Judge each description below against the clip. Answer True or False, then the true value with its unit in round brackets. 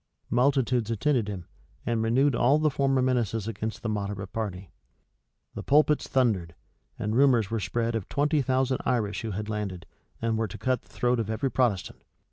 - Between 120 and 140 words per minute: False (175 wpm)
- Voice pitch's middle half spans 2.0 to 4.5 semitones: True (3.7 semitones)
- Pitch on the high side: False (115 Hz)